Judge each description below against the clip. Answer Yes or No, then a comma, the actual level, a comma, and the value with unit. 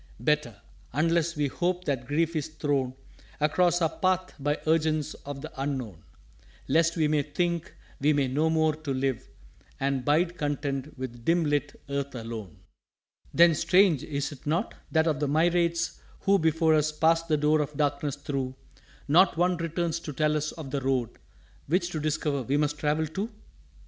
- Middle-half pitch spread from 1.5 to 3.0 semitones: Yes, average, 2.7 semitones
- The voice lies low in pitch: No, medium, 150 Hz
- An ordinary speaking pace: Yes, average, 170 wpm